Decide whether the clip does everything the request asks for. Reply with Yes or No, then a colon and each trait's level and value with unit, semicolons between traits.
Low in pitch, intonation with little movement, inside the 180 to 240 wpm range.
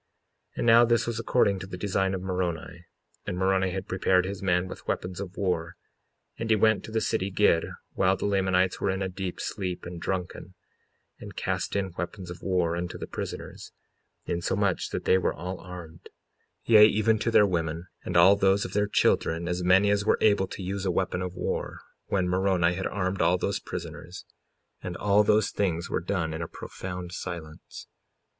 Yes: very low, 95 Hz; narrow, 2.1 semitones; average, 195 wpm